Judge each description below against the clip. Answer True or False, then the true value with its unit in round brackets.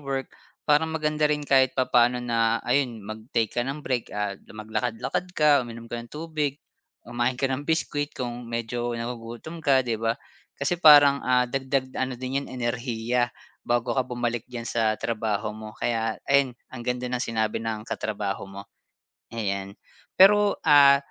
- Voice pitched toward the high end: False (125 Hz)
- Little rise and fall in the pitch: False (3.2 semitones)